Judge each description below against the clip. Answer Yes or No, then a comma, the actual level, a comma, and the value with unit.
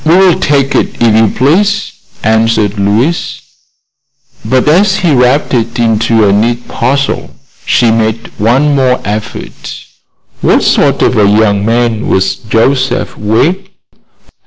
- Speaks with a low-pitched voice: Yes, low, 120 Hz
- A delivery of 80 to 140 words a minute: Yes, slow, 135 wpm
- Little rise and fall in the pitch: No, average, 4.4 semitones